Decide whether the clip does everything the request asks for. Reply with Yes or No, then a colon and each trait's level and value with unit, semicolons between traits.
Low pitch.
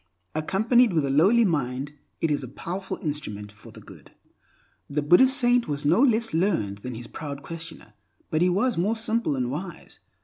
No: medium, 160 Hz